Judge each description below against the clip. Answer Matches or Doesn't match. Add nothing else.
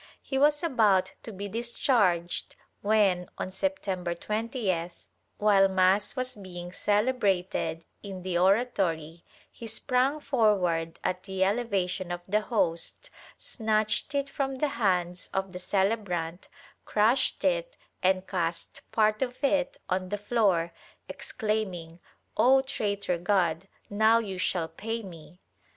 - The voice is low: Doesn't match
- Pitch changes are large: Doesn't match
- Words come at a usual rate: Doesn't match